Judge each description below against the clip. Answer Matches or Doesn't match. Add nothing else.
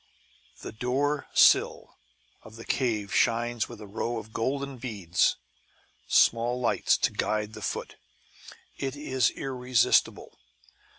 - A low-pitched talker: Matches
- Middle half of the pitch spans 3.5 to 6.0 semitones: Doesn't match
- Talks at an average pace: Doesn't match